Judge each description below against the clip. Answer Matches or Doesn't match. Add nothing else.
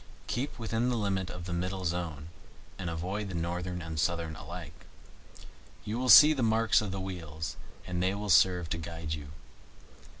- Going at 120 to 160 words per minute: Doesn't match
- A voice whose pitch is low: Matches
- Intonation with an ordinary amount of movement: Matches